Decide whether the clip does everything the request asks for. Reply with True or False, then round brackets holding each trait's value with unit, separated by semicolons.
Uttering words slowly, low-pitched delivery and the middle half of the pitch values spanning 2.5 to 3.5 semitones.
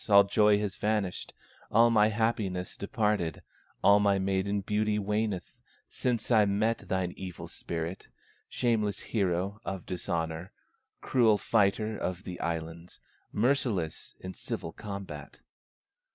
True (120 wpm; 100 Hz; 2.9 semitones)